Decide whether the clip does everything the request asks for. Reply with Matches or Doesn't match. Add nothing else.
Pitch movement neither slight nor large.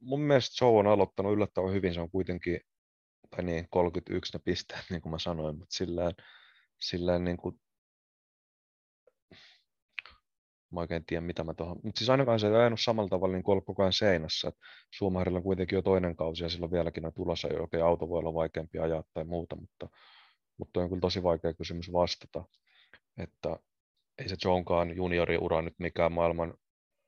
Doesn't match